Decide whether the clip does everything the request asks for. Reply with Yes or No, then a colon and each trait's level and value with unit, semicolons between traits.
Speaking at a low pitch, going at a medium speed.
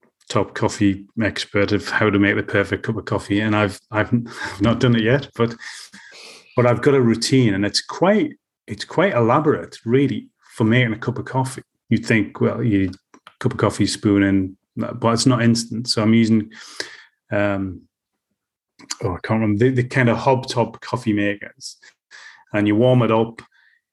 Yes: low, 115 Hz; average, 185 wpm